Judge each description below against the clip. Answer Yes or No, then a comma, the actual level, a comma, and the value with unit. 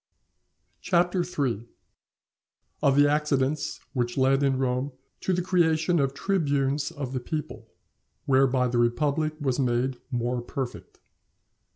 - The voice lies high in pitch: No, low, 135 Hz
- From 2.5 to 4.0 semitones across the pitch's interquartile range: Yes, average, 3.3 semitones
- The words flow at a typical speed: No, slow, 115 wpm